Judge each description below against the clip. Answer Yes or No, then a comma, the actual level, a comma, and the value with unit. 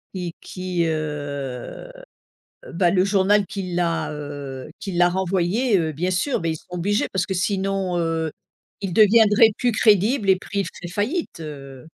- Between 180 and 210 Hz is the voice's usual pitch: Yes, medium, 185 Hz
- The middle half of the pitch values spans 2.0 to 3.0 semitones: No, average, 3.8 semitones